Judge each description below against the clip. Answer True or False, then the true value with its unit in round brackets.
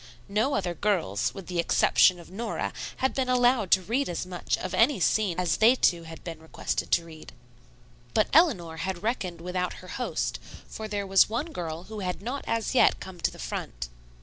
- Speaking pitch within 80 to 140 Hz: False (185 Hz)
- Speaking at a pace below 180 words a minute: False (200 wpm)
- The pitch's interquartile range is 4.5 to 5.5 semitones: True (4.9 semitones)